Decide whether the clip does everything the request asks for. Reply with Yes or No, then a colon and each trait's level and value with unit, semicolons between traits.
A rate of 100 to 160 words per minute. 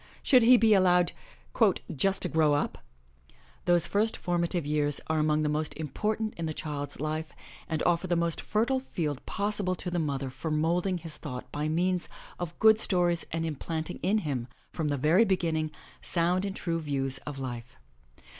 No: average, 180 wpm